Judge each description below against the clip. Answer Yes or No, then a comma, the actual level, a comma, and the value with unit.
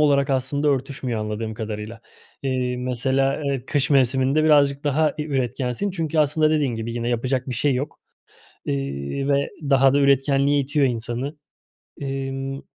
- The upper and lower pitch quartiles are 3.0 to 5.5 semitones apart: No, narrow, 2.5 semitones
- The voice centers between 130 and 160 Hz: Yes, low, 135 Hz